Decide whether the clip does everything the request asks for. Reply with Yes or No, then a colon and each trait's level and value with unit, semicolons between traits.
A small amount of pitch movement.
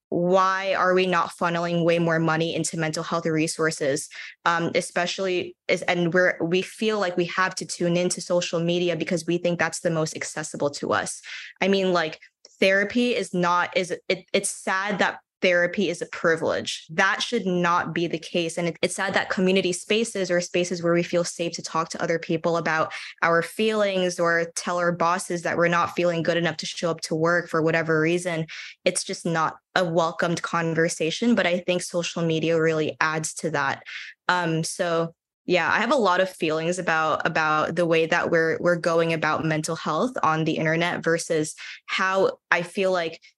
Yes: narrow, 1.8 semitones